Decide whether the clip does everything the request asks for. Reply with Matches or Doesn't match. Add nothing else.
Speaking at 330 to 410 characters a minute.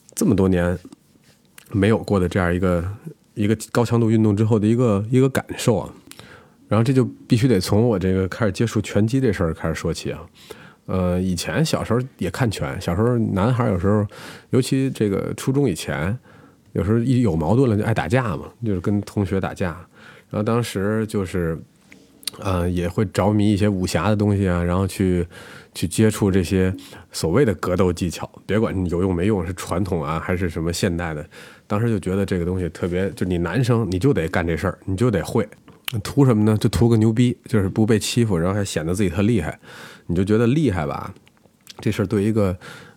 Doesn't match